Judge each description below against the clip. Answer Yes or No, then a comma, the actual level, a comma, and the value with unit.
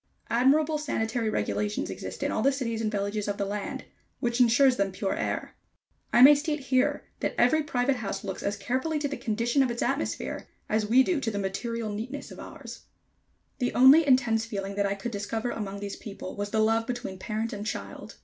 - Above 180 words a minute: Yes, fast, 205 wpm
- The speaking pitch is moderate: No, high, 230 Hz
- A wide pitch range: No, average, 4.1 semitones